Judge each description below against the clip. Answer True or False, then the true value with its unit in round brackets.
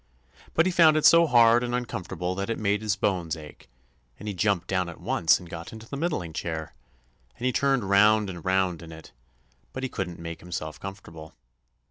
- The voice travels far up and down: True (5.8 semitones)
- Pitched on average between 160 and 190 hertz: False (95 Hz)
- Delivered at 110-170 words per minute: False (200 wpm)